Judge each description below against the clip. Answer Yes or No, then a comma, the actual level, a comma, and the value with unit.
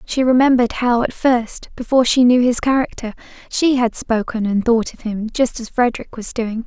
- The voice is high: Yes, high, 240 Hz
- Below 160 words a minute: No, average, 200 wpm